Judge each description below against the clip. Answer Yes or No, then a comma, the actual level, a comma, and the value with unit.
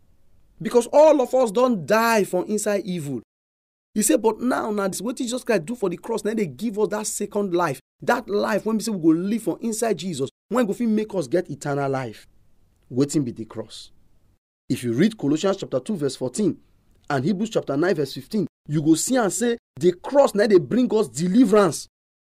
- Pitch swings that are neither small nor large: No, wide, 8.2 semitones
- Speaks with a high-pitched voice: Yes, high, 195 Hz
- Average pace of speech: No, fast, 210 wpm